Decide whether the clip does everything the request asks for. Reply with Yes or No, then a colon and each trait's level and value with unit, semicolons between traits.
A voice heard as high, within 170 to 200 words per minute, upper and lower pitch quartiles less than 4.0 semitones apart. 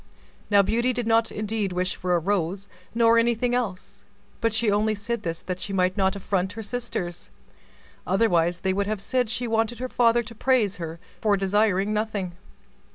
Yes: high, 205 Hz; average, 180 wpm; average, 3.3 semitones